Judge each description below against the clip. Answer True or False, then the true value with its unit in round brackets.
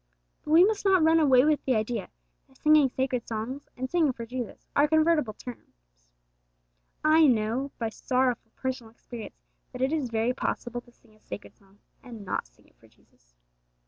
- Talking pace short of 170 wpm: False (180 wpm)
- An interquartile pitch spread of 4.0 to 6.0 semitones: True (4.7 semitones)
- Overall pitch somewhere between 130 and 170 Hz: False (255 Hz)